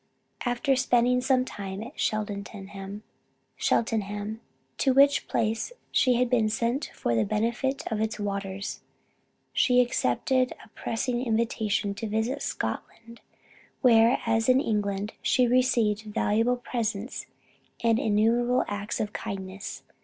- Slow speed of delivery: Yes, slow, 120 wpm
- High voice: Yes, high, 225 Hz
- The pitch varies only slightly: No, average, 3.1 semitones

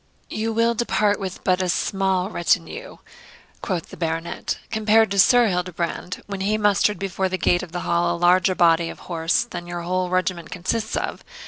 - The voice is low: No, medium, 185 Hz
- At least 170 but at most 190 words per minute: Yes, average, 185 wpm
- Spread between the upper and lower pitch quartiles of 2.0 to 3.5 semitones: Yes, average, 3.1 semitones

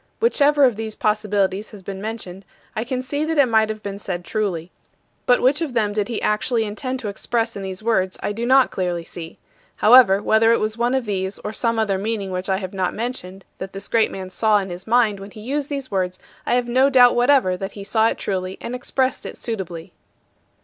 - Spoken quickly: Yes, fast, 225 wpm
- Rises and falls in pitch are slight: No, average, 4.0 semitones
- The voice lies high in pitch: Yes, high, 215 Hz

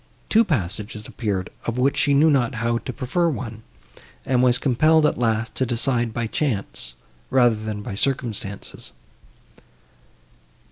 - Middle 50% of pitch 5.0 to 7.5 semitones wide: No, average, 3.5 semitones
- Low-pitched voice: Yes, low, 120 Hz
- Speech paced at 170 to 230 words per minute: No, average, 140 wpm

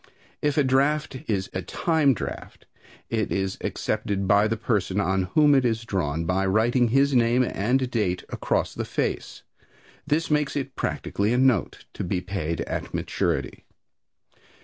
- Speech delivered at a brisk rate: No, average, 155 wpm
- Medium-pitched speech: No, low, 115 Hz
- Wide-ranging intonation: Yes, wide, 5.7 semitones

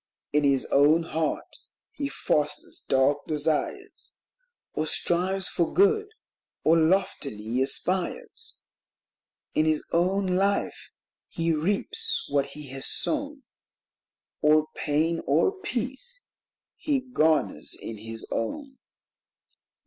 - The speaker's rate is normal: No, slow, 105 wpm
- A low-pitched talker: No, medium, 165 Hz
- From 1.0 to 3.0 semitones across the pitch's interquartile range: No, wide, 5.6 semitones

